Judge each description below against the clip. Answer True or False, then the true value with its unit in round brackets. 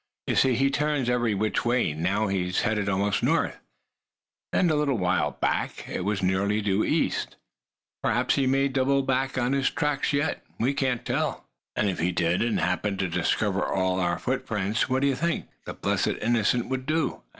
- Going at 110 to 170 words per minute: False (180 wpm)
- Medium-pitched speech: False (115 Hz)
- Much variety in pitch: True (5.8 semitones)